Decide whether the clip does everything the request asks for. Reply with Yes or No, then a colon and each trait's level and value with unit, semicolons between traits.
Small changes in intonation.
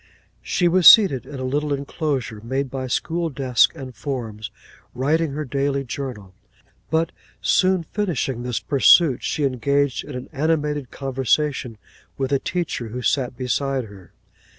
No: average, 3.1 semitones